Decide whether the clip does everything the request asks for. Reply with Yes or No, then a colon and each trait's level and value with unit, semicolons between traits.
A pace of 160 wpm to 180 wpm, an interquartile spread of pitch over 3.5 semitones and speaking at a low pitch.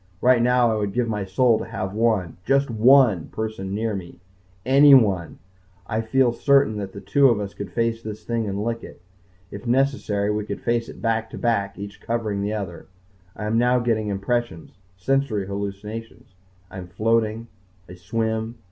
No: average, 175 wpm; average, 2.8 semitones; low, 110 Hz